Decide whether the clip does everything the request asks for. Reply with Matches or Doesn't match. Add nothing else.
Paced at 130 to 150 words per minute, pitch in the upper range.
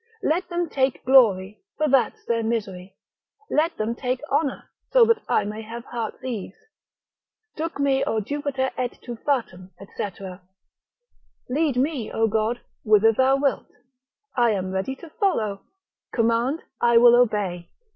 Matches